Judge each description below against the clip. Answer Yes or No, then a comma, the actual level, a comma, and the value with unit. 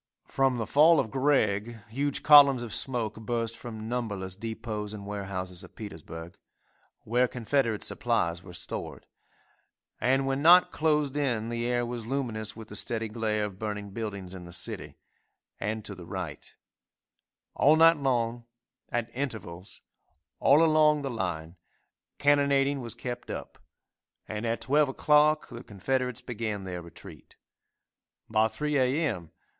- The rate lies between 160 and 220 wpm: No, average, 145 wpm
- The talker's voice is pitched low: Yes, low, 115 Hz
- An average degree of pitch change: Yes, average, 4.7 semitones